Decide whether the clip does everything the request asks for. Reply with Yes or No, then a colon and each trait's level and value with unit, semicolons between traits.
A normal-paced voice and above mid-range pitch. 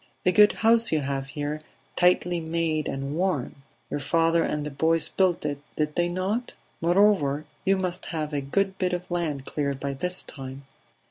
No: average, 180 wpm; medium, 165 Hz